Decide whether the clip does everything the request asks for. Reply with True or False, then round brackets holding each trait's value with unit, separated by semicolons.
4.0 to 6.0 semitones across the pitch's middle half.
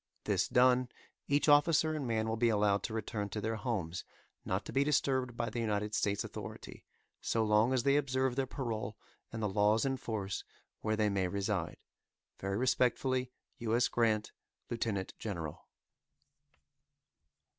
False (3.5 semitones)